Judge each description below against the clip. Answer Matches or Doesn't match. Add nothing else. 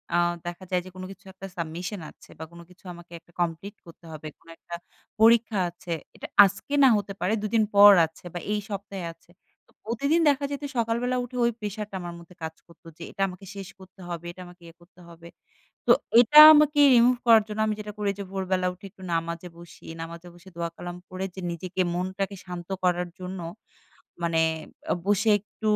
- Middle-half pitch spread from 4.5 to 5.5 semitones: Doesn't match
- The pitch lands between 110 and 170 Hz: Doesn't match